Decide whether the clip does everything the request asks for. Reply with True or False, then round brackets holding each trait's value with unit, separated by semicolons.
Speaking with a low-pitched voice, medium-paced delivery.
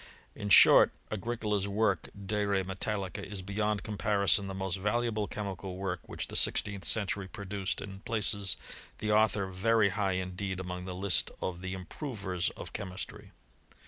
True (100 Hz; 150 wpm)